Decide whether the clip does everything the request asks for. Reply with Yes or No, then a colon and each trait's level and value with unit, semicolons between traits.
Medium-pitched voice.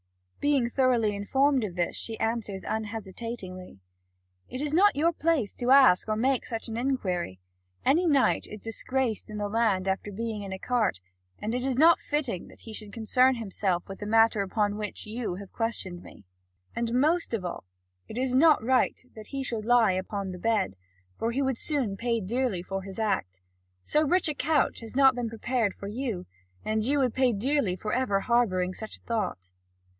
No: high, 225 Hz